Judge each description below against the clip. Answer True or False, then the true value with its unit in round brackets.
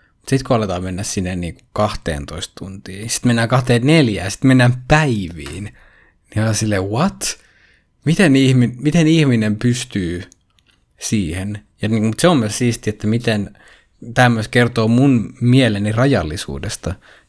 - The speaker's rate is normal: True (130 wpm)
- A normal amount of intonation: True (4.3 semitones)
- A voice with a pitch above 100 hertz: True (110 Hz)